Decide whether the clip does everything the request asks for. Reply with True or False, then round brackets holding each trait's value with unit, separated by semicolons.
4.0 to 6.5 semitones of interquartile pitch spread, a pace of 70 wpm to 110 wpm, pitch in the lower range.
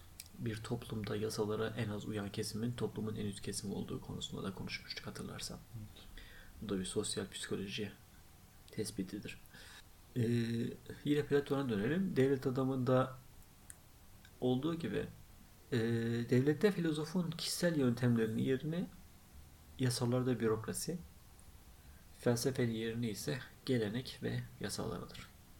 True (4.4 semitones; 105 wpm; 110 Hz)